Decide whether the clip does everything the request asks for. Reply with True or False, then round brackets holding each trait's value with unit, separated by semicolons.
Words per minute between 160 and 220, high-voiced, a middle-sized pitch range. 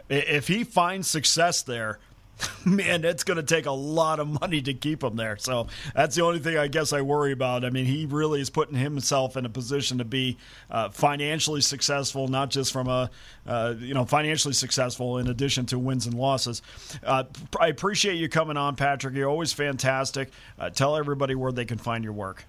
False (205 wpm; 135 Hz; 3.3 semitones)